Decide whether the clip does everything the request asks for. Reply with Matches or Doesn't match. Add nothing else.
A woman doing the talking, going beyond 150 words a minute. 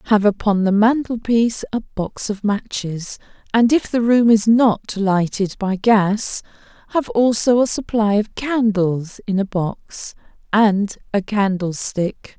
Doesn't match